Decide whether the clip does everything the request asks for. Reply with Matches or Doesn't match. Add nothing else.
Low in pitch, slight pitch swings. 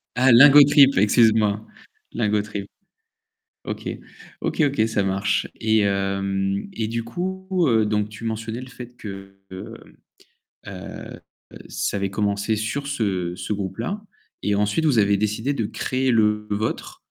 Doesn't match